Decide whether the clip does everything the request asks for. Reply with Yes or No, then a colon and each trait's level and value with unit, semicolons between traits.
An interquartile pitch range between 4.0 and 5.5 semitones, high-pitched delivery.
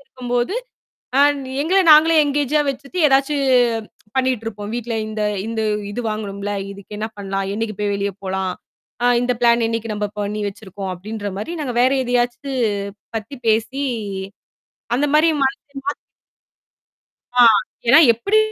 Yes: average, 4.7 semitones; high, 230 Hz